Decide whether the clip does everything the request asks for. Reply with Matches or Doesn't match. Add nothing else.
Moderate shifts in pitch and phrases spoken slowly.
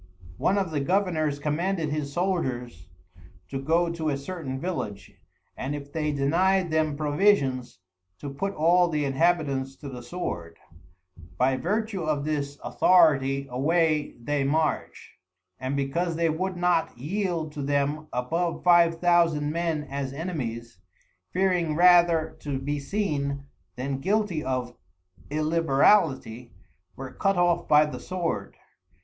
Matches